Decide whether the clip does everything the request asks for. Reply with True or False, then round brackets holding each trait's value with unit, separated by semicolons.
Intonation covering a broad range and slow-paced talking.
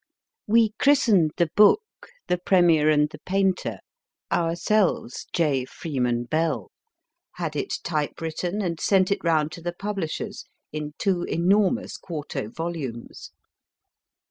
False (4.0 semitones; 120 wpm)